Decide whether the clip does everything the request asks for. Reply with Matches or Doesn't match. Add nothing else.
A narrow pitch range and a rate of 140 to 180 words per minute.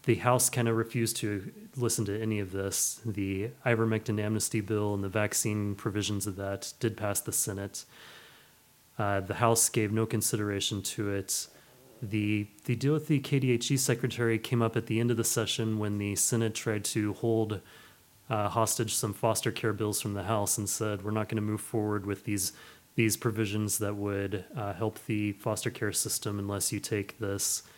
Doesn't match